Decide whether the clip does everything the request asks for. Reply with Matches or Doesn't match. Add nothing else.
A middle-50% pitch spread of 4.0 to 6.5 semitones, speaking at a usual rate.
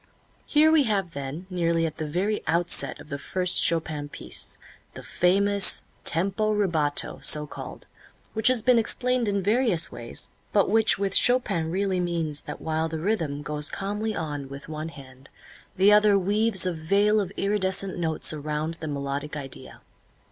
Matches